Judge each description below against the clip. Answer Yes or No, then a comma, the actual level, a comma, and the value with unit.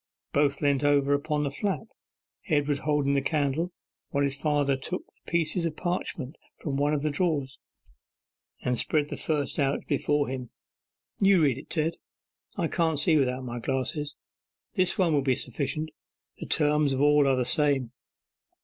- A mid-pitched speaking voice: Yes, medium, 145 Hz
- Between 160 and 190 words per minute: Yes, average, 165 wpm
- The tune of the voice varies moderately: No, narrow, 2.0 semitones